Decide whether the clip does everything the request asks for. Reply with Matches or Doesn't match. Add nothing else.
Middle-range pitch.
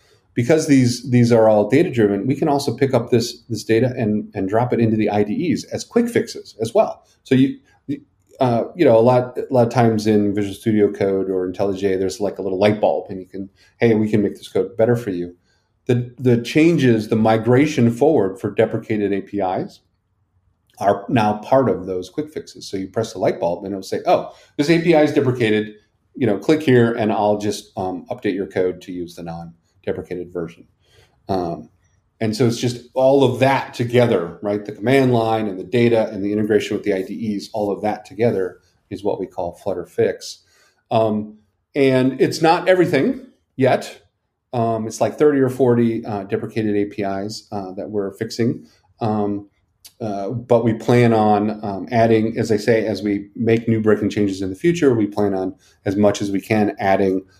Doesn't match